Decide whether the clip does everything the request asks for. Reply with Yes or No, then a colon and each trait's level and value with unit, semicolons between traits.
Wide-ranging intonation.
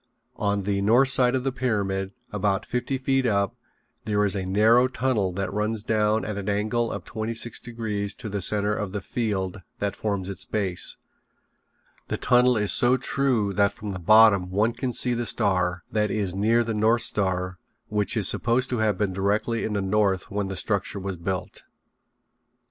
No: average, 2.9 semitones